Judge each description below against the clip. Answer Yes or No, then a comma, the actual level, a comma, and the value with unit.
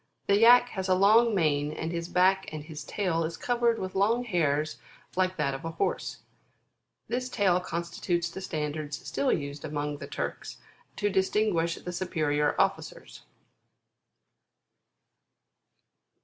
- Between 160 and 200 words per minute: No, slow, 135 wpm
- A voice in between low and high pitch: Yes, medium, 175 Hz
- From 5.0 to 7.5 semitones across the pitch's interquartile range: No, average, 4.6 semitones